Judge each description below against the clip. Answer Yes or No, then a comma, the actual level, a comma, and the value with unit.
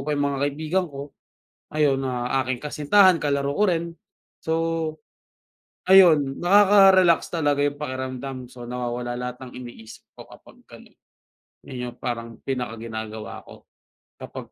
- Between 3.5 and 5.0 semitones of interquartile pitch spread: Yes, average, 4.2 semitones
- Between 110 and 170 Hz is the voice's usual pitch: Yes, medium, 140 Hz